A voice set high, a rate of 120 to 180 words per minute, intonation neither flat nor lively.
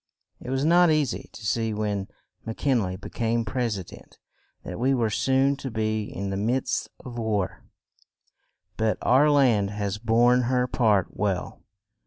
No: low, 115 Hz; average, 175 wpm; average, 3.7 semitones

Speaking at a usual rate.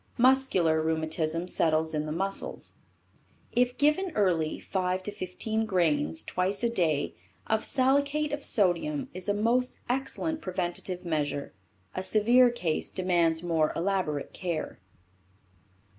No: slow, 125 wpm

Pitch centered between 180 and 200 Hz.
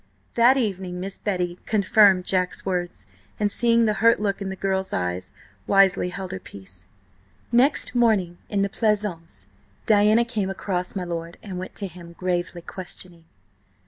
Yes: high, 190 Hz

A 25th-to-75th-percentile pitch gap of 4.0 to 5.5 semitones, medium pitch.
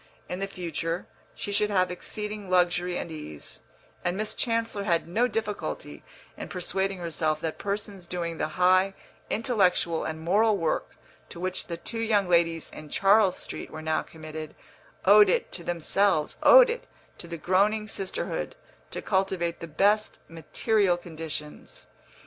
No: average, 3.5 semitones; medium, 180 Hz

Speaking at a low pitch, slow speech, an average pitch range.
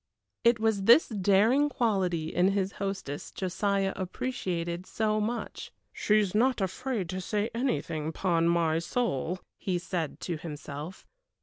No: high, 190 Hz; slow, 130 wpm; average, 4.2 semitones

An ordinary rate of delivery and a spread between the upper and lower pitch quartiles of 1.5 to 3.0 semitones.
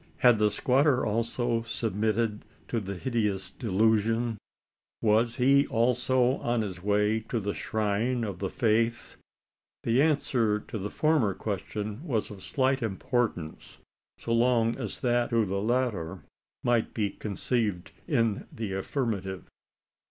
No: slow, 130 wpm; average, 2.7 semitones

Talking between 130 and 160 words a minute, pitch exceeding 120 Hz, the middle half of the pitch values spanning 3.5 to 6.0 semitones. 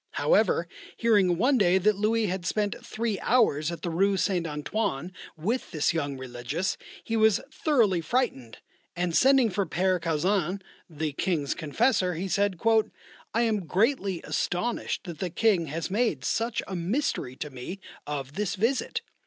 Yes: average, 155 wpm; medium, 185 Hz; average, 5.2 semitones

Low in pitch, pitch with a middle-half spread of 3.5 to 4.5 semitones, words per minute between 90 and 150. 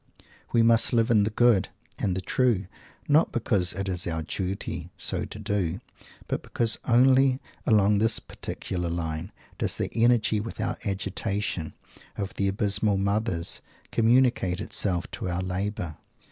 Yes: low, 100 Hz; average, 3.8 semitones; average, 145 wpm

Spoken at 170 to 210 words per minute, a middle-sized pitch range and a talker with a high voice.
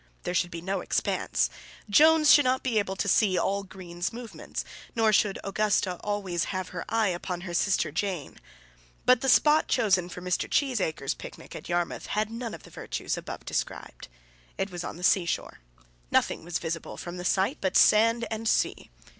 Yes: average, 180 wpm; average, 4.1 semitones; high, 195 Hz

